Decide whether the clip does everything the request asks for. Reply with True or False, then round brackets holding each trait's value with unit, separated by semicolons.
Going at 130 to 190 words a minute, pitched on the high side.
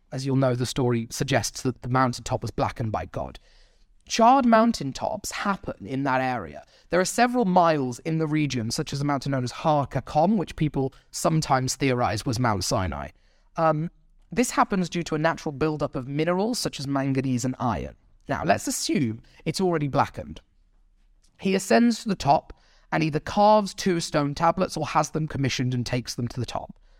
False (180 wpm; 140 Hz)